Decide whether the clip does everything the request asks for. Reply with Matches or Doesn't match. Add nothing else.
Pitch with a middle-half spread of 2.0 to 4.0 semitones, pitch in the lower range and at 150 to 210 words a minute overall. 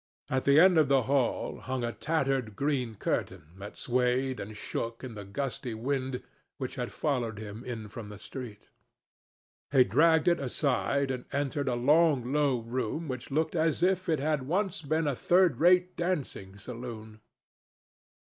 Doesn't match